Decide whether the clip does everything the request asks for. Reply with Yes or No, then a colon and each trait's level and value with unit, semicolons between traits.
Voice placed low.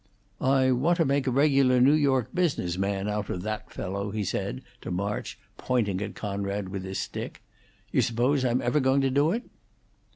Yes: low, 120 Hz